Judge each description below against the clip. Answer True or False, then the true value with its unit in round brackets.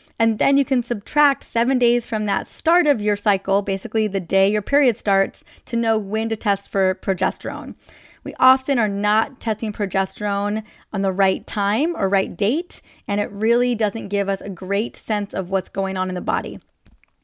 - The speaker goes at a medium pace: True (190 wpm)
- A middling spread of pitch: True (3.4 semitones)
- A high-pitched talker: True (210 Hz)